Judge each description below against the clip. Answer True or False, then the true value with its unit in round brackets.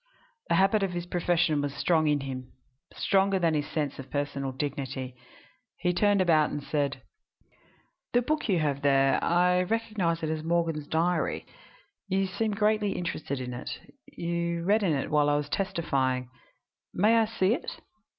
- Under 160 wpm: False (170 wpm)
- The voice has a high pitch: False (170 Hz)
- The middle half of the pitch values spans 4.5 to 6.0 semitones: True (5.0 semitones)